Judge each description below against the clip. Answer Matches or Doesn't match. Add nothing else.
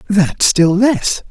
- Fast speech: Doesn't match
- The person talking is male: Matches